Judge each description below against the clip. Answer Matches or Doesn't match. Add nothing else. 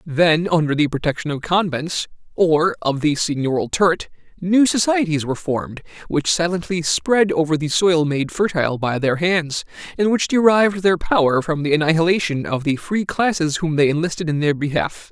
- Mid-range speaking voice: Matches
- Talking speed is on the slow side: Doesn't match